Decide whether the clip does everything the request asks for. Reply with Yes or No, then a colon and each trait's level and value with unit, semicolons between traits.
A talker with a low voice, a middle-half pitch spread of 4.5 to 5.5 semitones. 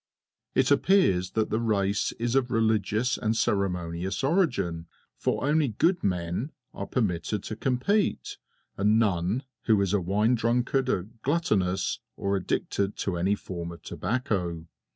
Yes: low, 105 Hz; average, 5.1 semitones